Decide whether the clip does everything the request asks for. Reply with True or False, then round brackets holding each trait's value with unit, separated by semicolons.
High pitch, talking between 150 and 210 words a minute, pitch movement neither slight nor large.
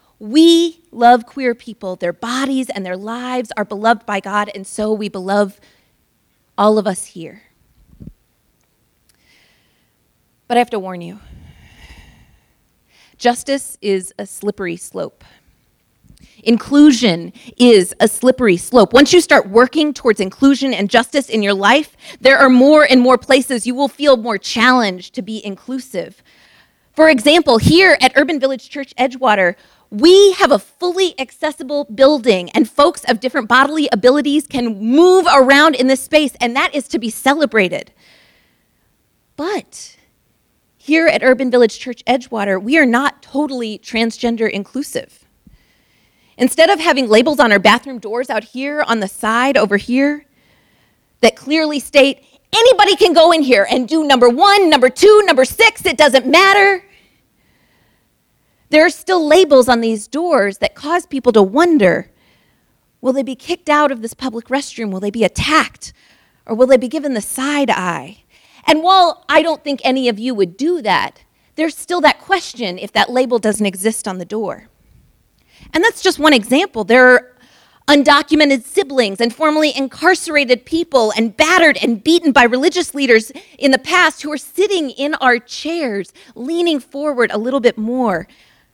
True (265 Hz; 155 wpm; 4.9 semitones)